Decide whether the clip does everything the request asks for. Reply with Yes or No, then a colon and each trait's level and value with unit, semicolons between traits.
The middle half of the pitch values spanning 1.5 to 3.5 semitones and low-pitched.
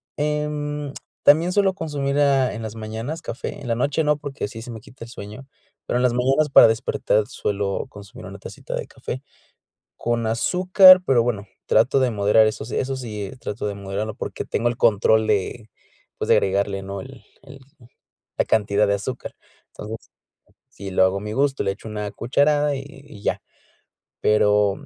No: average, 5.1 semitones; low, 115 Hz